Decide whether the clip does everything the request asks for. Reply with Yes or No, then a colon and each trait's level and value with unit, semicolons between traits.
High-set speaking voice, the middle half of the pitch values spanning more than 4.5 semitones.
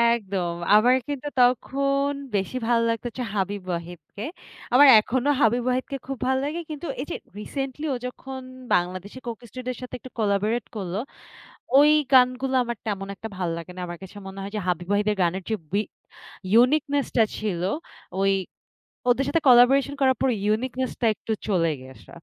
Yes: high, 235 Hz; average, 5.0 semitones